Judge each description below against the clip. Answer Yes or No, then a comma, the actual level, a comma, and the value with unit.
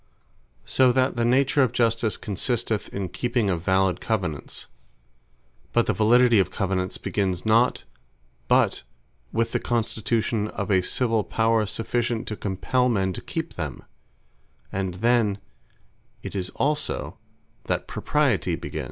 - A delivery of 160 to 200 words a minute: No, slow, 135 wpm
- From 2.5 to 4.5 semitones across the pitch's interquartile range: Yes, average, 3.7 semitones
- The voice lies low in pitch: Yes, low, 110 Hz